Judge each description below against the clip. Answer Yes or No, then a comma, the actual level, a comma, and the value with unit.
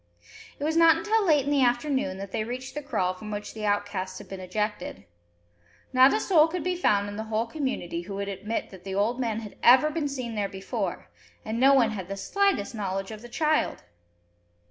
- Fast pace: Yes, fast, 215 wpm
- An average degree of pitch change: No, wide, 6.1 semitones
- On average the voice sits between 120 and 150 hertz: No, high, 225 Hz